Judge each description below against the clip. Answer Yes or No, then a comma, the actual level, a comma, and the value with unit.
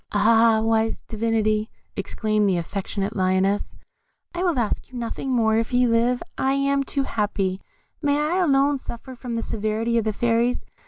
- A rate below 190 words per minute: Yes, average, 165 wpm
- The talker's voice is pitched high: Yes, high, 230 Hz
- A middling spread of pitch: Yes, average, 3.2 semitones